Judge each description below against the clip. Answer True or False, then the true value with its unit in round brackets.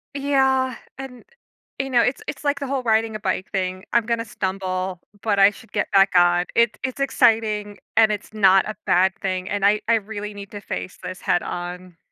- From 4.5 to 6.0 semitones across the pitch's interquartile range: False (3.7 semitones)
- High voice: True (210 Hz)